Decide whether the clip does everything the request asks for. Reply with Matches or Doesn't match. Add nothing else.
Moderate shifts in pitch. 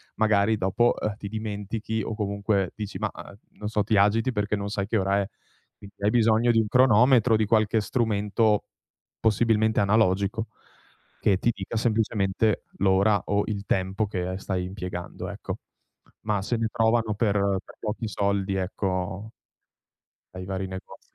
Doesn't match